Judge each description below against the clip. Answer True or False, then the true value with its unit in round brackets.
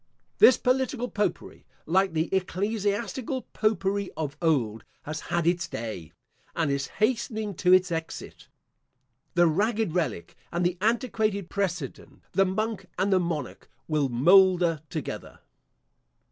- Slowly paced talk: True (125 wpm)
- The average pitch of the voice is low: False (185 Hz)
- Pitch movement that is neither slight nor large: True (4.4 semitones)